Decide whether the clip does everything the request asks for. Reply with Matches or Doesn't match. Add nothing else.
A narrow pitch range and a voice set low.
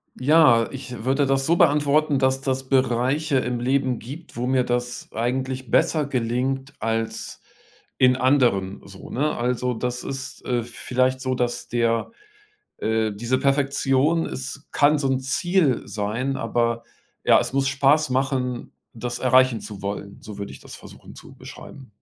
Matches